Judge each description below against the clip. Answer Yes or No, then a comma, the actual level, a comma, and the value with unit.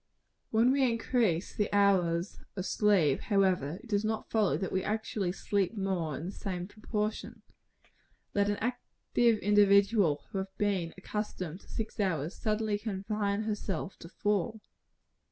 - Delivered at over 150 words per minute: No, average, 145 wpm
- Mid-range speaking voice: No, high, 205 Hz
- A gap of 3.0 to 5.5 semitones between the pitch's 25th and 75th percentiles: No, narrow, 2.5 semitones